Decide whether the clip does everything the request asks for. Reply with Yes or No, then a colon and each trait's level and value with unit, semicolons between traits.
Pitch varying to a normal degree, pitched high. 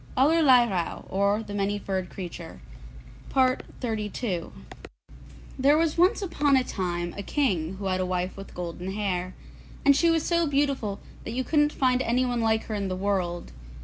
No: wide, 6.5 semitones; high, 215 Hz